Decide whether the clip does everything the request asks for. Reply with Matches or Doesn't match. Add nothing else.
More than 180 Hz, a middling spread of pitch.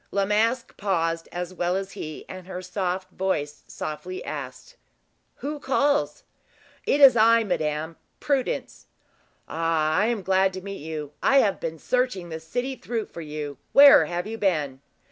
Doesn't match